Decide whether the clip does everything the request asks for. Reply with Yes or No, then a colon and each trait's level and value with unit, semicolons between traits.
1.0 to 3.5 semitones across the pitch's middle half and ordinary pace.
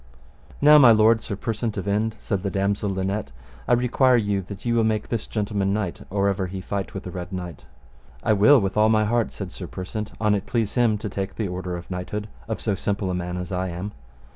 No: narrow, 2.6 semitones; fast, 235 wpm